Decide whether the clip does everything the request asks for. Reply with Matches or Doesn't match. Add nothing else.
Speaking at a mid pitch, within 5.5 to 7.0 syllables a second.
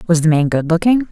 Matches